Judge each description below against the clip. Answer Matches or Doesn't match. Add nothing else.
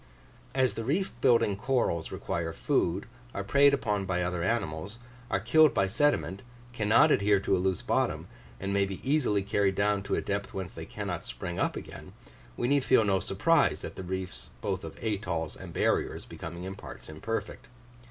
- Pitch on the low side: Matches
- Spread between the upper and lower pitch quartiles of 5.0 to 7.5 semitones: Doesn't match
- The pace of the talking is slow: Doesn't match